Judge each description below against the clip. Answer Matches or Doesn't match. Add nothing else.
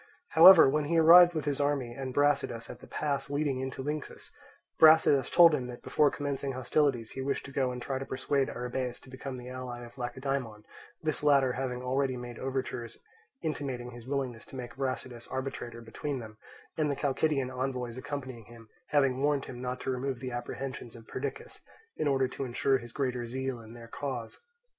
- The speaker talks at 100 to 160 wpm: Doesn't match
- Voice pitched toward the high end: Doesn't match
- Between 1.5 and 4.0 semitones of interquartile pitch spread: Matches